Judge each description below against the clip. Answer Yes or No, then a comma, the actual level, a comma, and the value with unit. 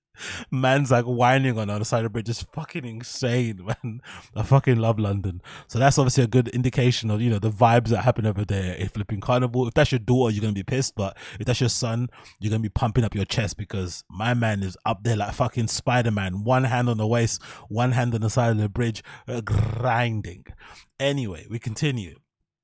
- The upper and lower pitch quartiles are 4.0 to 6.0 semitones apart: No, average, 2.7 semitones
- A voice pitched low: Yes, low, 115 Hz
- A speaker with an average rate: No, fast, 225 wpm